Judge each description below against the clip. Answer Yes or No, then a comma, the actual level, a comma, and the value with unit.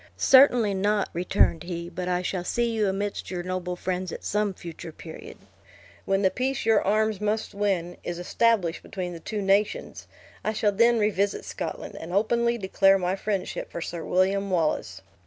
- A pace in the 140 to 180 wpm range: Yes, average, 175 wpm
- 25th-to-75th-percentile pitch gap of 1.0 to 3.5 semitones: Yes, average, 3.1 semitones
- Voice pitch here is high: Yes, high, 195 Hz